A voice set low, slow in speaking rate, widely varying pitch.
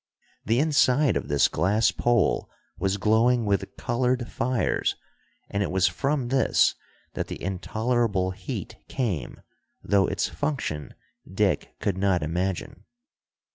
No: low, 105 Hz; slow, 125 wpm; average, 4.8 semitones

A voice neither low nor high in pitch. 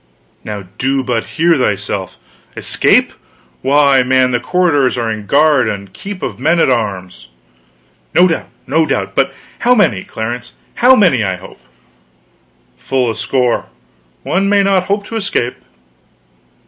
No: low, 130 Hz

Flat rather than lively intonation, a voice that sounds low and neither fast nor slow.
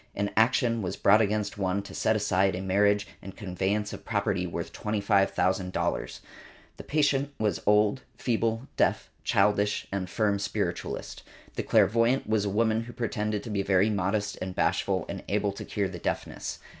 Yes: narrow, 2.1 semitones; low, 105 Hz; average, 170 wpm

